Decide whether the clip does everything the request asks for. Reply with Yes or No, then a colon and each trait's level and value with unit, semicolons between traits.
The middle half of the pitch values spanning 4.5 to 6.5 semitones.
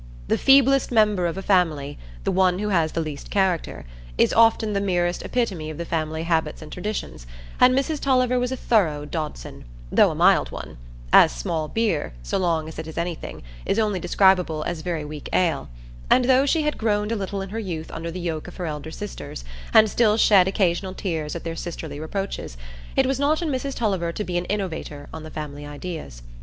Yes: average, 5.1 semitones